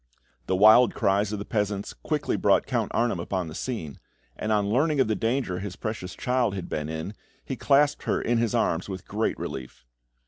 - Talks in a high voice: No, low, 105 Hz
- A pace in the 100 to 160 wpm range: No, average, 200 wpm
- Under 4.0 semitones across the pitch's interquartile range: No, average, 4.4 semitones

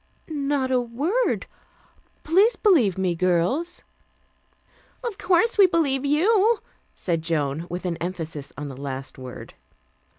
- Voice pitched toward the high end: Yes, very high, 250 Hz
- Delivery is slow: Yes, slow, 125 wpm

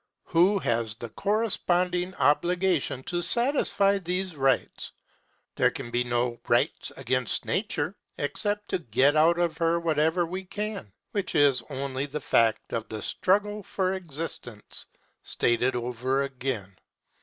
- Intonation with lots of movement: Yes, wide, 6.7 semitones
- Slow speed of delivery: Yes, slow, 130 wpm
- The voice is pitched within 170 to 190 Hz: No, medium, 160 Hz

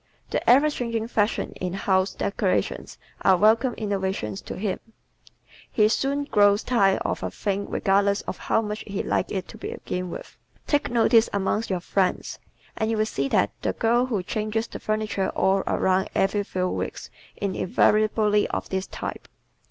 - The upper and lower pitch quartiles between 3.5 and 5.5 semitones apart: No, average, 2.7 semitones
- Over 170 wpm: No, average, 165 wpm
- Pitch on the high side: Yes, high, 205 Hz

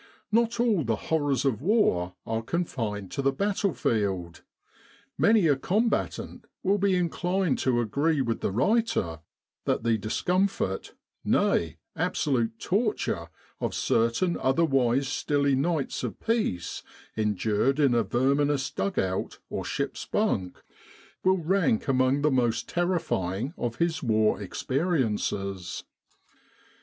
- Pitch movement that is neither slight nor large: No, wide, 8.0 semitones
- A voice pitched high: No, low, 135 Hz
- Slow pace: Yes, slow, 120 wpm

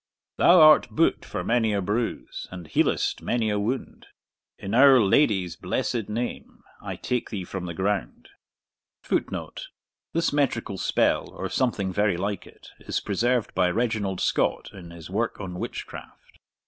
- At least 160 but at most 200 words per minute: No, average, 150 wpm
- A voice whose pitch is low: Yes, low, 105 Hz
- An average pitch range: Yes, average, 4.4 semitones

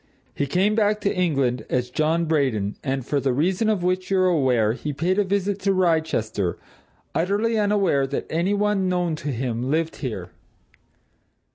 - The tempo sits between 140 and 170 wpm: Yes, average, 165 wpm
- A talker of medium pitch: Yes, medium, 165 Hz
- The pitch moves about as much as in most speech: No, wide, 6.3 semitones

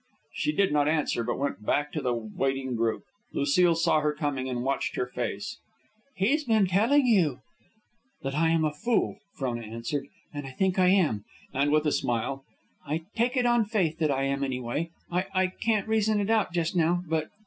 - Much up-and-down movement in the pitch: Yes, wide, 6.4 semitones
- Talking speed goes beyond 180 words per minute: Yes, average, 200 wpm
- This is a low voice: No, medium, 155 Hz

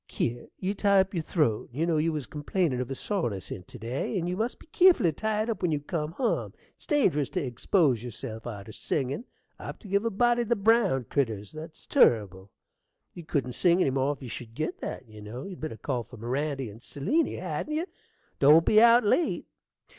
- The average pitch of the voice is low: No, medium, 155 Hz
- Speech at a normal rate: No, fast, 220 wpm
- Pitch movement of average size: No, wide, 8.1 semitones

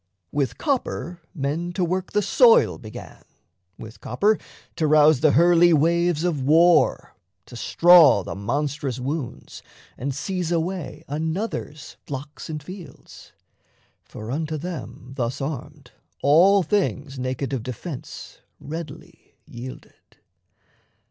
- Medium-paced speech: No, slow, 115 wpm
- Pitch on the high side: No, medium, 155 Hz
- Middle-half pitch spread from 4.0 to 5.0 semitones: Yes, average, 4.3 semitones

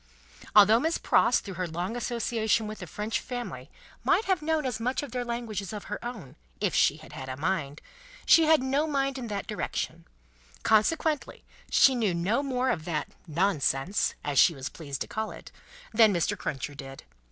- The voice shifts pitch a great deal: Yes, wide, 6.6 semitones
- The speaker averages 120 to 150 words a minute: No, average, 190 wpm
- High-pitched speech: Yes, high, 215 Hz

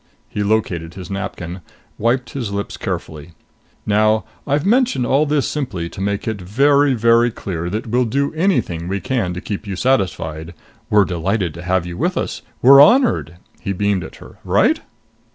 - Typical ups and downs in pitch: No, wide, 6.4 semitones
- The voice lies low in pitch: Yes, low, 105 Hz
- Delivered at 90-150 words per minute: No, average, 175 wpm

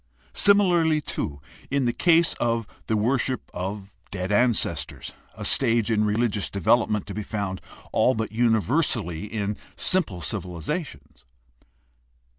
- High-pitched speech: No, low, 110 Hz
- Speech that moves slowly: Yes, slow, 120 wpm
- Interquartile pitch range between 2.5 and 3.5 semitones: No, average, 4.3 semitones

